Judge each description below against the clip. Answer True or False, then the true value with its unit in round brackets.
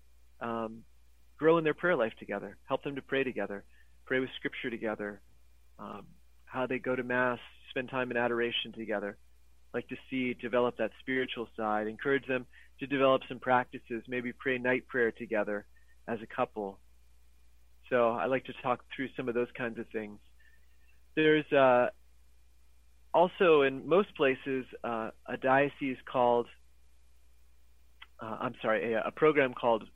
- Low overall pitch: True (115 Hz)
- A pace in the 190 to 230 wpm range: False (155 wpm)